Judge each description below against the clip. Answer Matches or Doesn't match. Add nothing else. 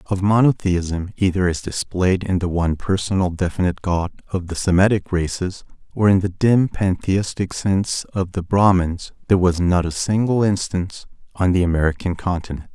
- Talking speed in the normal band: Matches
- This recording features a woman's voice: Doesn't match